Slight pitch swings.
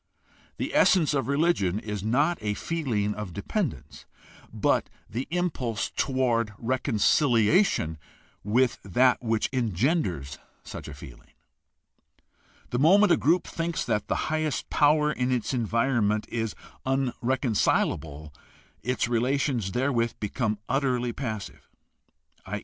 No: average, 4.9 semitones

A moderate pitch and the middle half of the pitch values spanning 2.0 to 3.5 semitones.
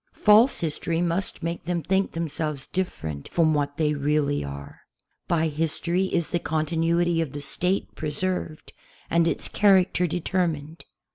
Yes: medium, 165 Hz; average, 2.8 semitones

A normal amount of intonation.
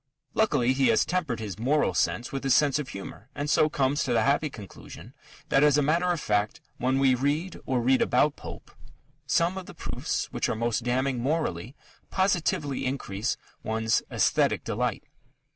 Yes: average, 4.0 semitones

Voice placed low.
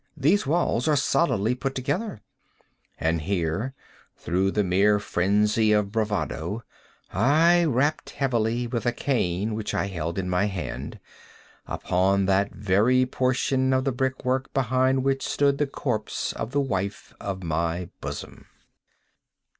Yes: low, 110 Hz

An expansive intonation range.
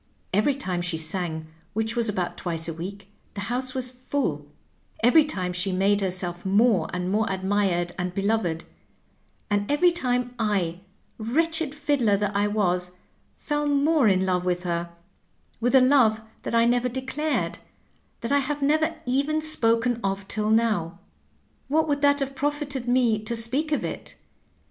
Yes: wide, 6.5 semitones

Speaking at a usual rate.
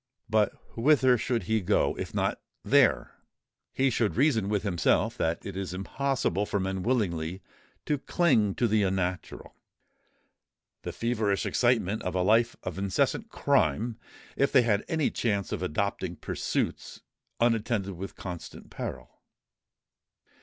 No: slow, 130 wpm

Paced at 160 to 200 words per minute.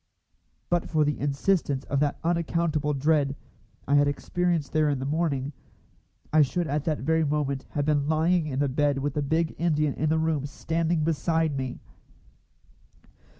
Yes: average, 165 wpm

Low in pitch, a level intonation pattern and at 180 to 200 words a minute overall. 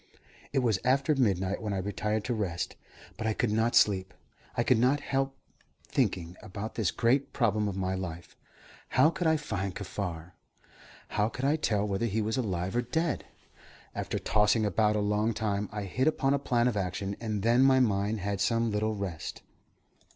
No: low, 105 Hz; average, 3.7 semitones; average, 185 wpm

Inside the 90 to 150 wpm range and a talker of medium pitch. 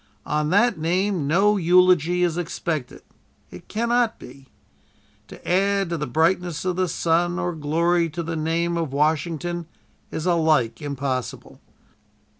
Yes: slow, 135 wpm; medium, 170 Hz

